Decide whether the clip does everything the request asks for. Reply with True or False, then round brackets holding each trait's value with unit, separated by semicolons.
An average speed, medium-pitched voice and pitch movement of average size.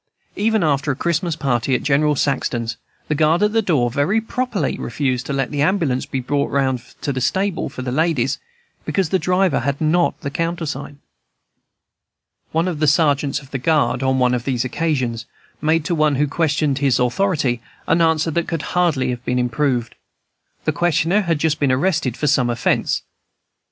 True (180 wpm; 145 Hz; 4.2 semitones)